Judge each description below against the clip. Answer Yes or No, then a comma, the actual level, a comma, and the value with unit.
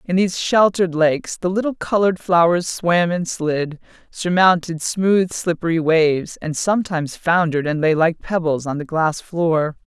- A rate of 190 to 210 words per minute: No, average, 160 wpm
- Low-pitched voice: No, medium, 170 Hz